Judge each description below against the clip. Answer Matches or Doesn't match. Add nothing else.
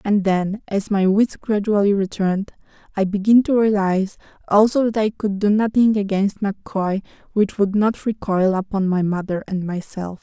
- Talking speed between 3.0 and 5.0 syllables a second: Matches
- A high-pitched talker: Matches